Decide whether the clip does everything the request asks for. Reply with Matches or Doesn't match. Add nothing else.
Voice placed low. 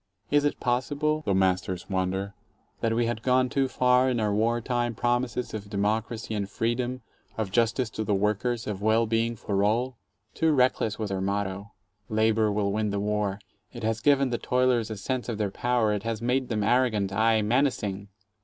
Matches